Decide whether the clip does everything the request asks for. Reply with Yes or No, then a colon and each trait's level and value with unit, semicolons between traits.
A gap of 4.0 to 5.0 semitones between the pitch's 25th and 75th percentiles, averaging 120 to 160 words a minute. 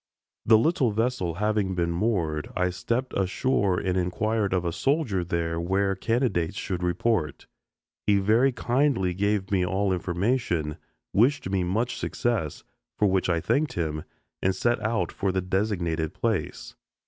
Yes: average, 4.3 semitones; average, 150 wpm